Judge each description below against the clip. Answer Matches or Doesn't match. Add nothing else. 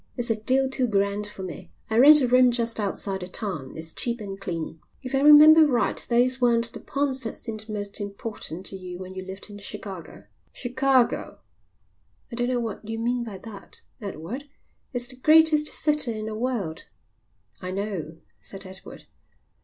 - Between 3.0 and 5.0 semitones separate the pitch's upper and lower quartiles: Matches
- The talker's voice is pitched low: Doesn't match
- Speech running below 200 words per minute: Matches